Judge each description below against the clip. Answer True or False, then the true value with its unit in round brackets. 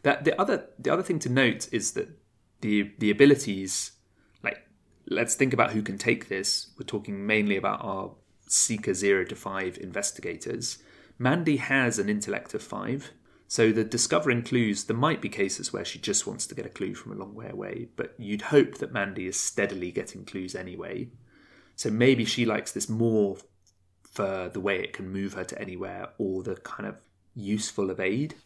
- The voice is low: True (105 Hz)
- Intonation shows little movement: False (3.9 semitones)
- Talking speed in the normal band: True (190 wpm)